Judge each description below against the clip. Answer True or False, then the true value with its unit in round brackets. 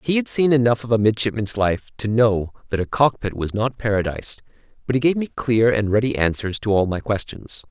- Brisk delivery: True (220 wpm)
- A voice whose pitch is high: False (110 Hz)